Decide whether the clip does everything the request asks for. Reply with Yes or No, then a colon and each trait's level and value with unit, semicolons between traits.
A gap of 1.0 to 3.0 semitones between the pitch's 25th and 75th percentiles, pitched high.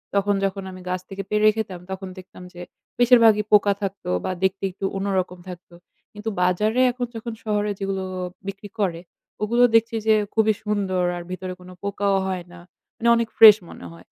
Yes: narrow, 2.6 semitones; high, 200 Hz